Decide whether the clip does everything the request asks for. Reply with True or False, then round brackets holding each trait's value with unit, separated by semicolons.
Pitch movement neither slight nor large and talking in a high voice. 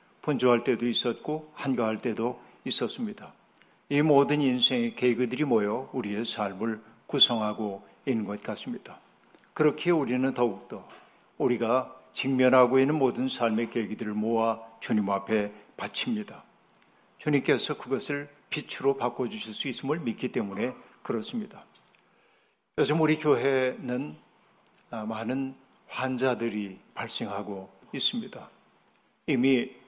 False (3.6 semitones; 125 Hz)